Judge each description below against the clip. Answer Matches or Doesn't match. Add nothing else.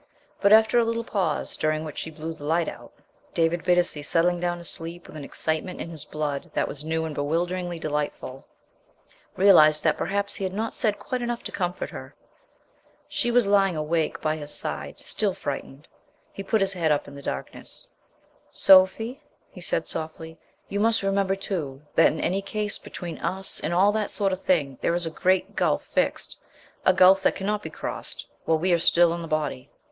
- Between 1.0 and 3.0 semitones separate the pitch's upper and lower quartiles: Doesn't match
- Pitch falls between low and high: Matches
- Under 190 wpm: Doesn't match